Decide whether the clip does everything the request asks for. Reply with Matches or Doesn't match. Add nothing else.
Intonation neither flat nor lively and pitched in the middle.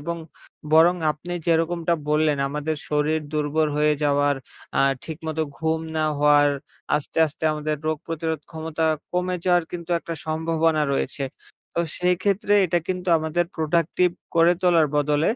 Doesn't match